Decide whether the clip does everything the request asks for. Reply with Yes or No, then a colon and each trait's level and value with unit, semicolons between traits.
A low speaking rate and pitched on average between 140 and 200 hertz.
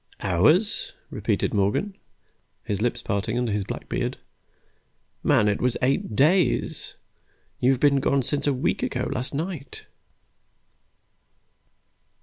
No: slow, 125 wpm; low, 130 Hz